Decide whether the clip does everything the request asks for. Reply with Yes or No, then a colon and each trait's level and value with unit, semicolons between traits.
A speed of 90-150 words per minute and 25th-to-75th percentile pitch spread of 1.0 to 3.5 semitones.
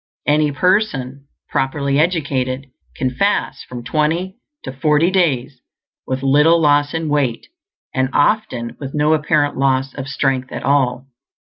Yes: slow, 135 wpm; average, 2.8 semitones